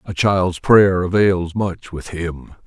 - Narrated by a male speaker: Yes, male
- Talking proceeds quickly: No, average, 155 wpm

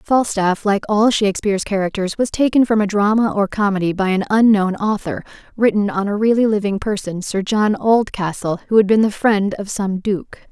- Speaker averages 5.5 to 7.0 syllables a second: No, 5.2 syllables/s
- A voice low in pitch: No, high, 205 Hz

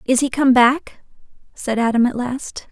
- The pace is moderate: Yes, average, 175 wpm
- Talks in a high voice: Yes, very high, 250 Hz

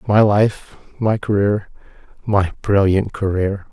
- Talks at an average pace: No, slow, 80 wpm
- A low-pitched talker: Yes, low, 100 Hz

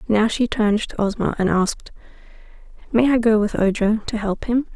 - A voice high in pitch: Yes, high, 220 Hz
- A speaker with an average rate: Yes, average, 190 wpm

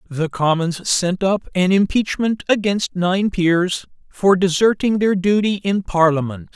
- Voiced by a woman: No, male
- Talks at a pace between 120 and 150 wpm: Yes, slow, 135 wpm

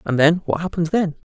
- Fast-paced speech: Yes, fast, 230 wpm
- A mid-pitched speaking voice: Yes, medium, 170 Hz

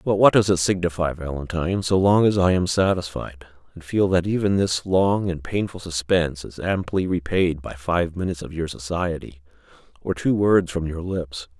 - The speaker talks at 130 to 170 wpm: No, average, 185 wpm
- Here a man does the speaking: Yes, male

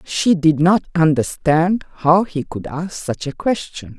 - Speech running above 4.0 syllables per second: No, 3.9 syllables/s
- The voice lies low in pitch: No, medium, 165 Hz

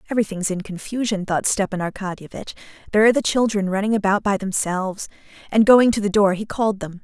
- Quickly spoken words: No, average, 190 wpm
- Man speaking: No, female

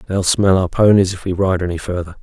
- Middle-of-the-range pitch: No, very low, 95 Hz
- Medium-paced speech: No, fast, 245 wpm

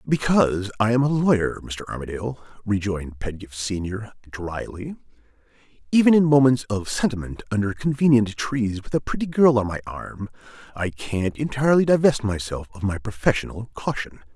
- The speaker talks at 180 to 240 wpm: No, average, 145 wpm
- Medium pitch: No, low, 110 Hz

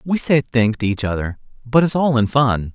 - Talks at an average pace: No, fast, 240 wpm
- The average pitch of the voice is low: Yes, low, 125 Hz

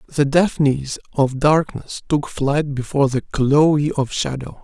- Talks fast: No, average, 140 wpm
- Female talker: No, male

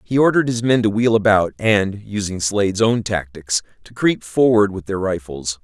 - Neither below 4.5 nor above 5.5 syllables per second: Yes, 5.0 syllables/s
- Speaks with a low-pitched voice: Yes, low, 105 Hz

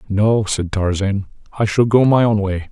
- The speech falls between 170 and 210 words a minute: Yes, average, 200 wpm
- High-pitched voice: No, low, 105 Hz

